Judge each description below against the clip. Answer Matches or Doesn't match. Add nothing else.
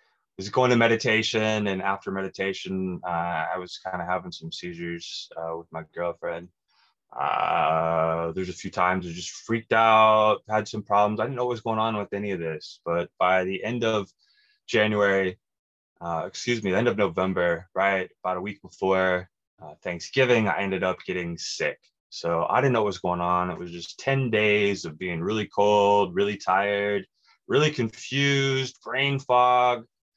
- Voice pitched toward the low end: Matches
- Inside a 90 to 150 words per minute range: Doesn't match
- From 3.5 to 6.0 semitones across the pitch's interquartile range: Matches